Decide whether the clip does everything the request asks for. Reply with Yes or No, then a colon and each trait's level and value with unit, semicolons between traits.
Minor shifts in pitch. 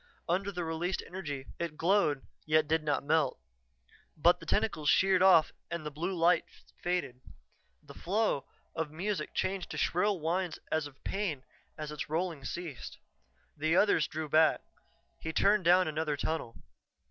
No: average, 3.2 semitones